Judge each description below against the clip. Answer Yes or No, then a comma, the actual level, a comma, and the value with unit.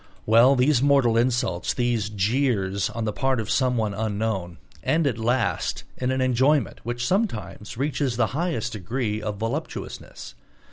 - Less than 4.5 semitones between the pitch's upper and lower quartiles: Yes, average, 3.5 semitones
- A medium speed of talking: Yes, average, 145 wpm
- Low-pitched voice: Yes, low, 120 Hz